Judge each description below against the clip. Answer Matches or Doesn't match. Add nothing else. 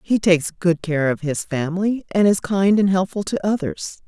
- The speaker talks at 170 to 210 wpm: Matches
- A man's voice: Doesn't match